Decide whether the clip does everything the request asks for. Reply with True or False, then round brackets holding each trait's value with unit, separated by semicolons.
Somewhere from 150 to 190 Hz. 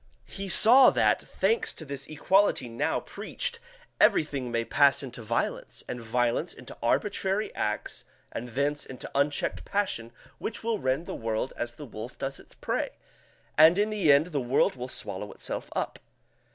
False (140 Hz)